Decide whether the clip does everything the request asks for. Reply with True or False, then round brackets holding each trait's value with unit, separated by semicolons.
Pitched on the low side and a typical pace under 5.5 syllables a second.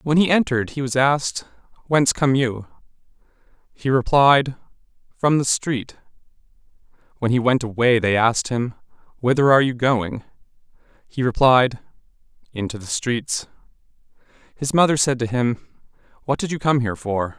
True (125 Hz; 5.0 syllables/s)